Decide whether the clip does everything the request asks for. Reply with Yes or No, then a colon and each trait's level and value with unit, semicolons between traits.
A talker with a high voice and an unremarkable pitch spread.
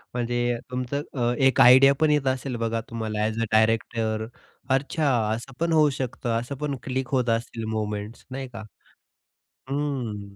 No: low, 120 Hz; average, 3.1 semitones